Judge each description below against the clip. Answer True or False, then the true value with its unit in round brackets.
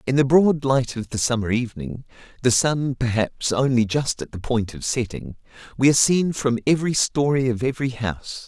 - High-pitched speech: False (125 Hz)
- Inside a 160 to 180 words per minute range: False (190 wpm)